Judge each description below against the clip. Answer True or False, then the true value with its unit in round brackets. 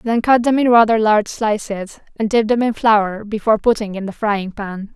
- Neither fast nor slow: False (220 wpm)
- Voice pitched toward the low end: False (215 Hz)